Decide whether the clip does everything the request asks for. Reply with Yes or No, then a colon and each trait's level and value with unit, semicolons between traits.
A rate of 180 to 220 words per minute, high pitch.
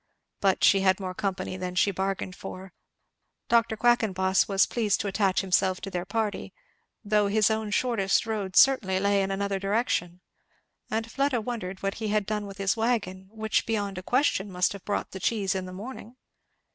Yes: average, 185 wpm; high, 200 Hz